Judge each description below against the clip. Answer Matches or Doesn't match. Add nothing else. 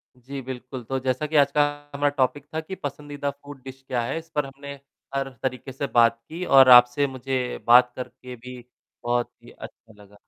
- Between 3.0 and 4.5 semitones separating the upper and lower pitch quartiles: Doesn't match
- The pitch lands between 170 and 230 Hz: Doesn't match